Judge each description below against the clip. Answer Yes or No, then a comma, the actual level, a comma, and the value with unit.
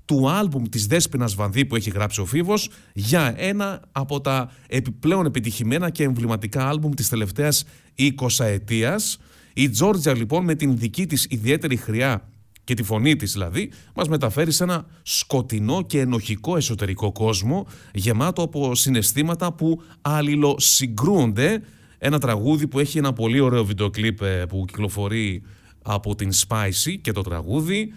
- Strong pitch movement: Yes, wide, 5.7 semitones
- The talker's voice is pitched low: Yes, low, 130 Hz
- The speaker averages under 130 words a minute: No, average, 145 wpm